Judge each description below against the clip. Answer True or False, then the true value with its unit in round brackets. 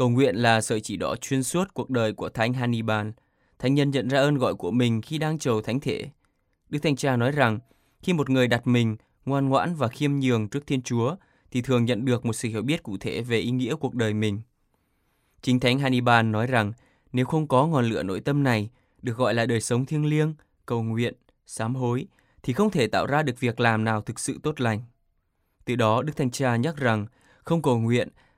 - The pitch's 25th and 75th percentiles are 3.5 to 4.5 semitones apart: False (3.1 semitones)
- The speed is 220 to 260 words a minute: True (225 wpm)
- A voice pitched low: True (125 Hz)